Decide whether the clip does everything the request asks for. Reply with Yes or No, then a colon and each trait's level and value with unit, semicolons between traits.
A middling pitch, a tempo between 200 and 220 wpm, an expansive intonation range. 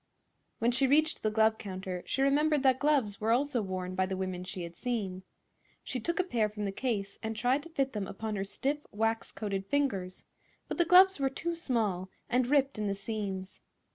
No: high, 220 Hz; fast, 205 wpm; wide, 5.9 semitones